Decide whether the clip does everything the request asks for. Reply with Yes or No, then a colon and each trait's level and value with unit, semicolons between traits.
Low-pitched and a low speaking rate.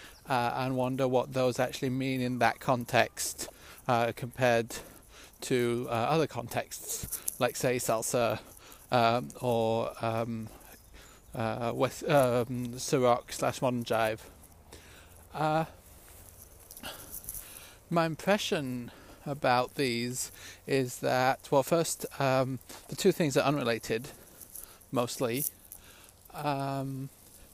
Yes: low, 120 Hz; slow, 100 wpm